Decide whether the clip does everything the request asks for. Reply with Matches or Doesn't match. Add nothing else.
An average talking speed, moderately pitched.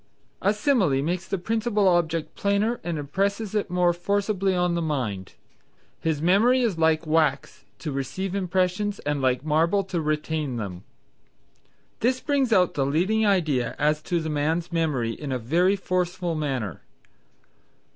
Matches